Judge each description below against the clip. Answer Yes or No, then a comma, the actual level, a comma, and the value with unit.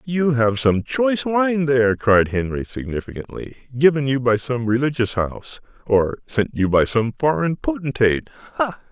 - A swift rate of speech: No, average, 155 wpm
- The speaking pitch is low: Yes, low, 125 Hz